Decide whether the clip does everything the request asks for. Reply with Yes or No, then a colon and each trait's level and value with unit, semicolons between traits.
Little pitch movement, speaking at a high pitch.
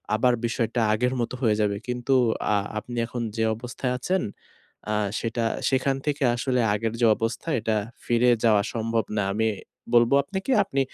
No: narrow, 2.1 semitones; low, 120 Hz